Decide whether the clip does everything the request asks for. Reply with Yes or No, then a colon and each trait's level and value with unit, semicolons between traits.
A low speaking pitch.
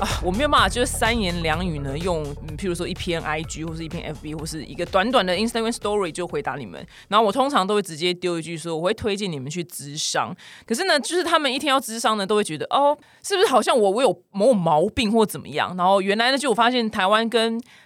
No: high, 195 Hz